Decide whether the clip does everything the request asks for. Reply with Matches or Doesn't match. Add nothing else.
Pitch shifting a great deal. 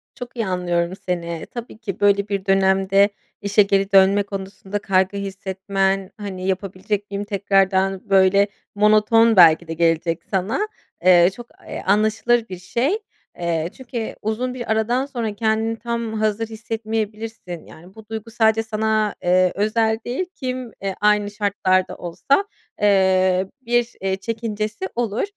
Doesn't match